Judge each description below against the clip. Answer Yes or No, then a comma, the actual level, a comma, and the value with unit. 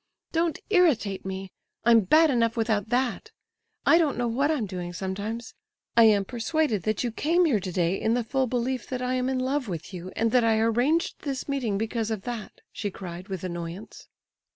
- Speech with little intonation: No, average, 4.7 semitones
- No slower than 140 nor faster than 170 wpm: No, average, 190 wpm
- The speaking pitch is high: Yes, high, 230 Hz